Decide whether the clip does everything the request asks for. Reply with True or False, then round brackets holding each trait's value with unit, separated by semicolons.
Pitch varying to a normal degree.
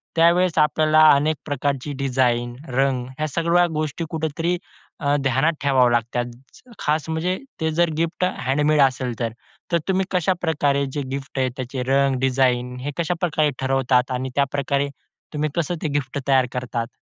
True (3.5 semitones)